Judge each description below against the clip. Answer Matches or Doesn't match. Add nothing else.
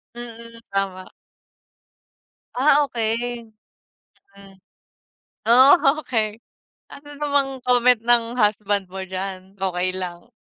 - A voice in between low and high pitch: Doesn't match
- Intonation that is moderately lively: Matches